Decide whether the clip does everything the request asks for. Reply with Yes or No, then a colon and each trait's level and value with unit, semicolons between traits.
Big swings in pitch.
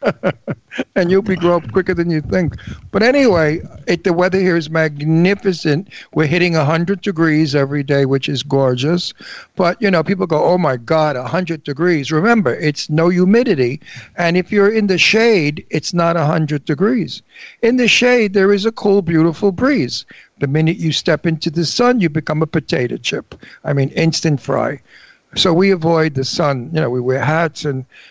No: average, 3.8 semitones